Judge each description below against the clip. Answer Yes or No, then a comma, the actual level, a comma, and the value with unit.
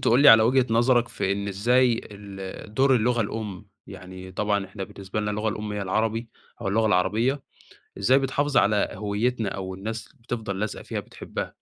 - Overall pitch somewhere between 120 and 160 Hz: No, low, 110 Hz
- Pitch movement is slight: No, average, 3.2 semitones